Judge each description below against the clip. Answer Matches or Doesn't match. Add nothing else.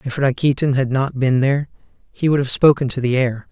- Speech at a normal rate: Doesn't match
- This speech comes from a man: Matches